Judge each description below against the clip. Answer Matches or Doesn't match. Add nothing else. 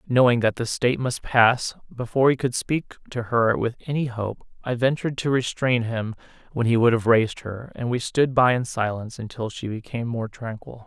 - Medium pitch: Doesn't match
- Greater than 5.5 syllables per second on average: Doesn't match